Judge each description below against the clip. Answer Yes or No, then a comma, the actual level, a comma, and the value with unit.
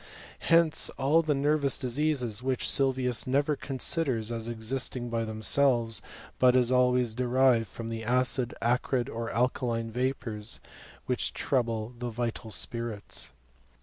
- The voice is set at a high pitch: No, low, 125 Hz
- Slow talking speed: Yes, slow, 130 wpm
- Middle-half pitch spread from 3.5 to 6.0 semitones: No, narrow, 2.5 semitones